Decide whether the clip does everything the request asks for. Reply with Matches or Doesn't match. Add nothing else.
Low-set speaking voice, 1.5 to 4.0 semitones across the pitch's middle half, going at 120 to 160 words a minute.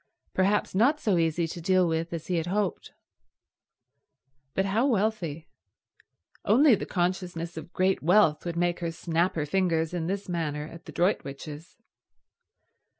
Doesn't match